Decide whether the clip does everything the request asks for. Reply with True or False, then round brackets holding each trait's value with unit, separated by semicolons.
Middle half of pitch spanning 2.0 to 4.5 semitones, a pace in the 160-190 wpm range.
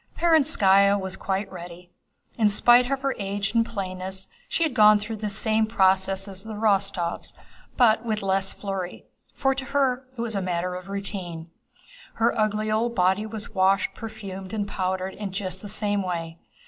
True (2.6 semitones; 170 wpm)